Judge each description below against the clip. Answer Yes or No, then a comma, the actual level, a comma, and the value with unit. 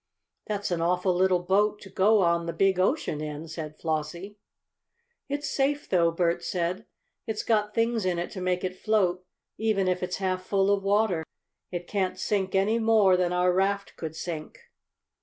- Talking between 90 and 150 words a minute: No, average, 175 wpm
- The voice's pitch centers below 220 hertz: Yes, medium, 185 Hz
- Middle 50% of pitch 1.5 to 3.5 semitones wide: Yes, average, 2.9 semitones